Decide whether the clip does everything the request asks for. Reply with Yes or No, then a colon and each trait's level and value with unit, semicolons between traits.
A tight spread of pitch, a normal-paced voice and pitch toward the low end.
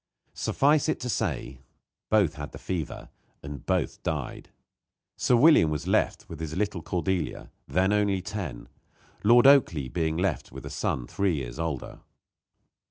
No: wide, 5.5 semitones; average, 150 wpm; very low, 90 Hz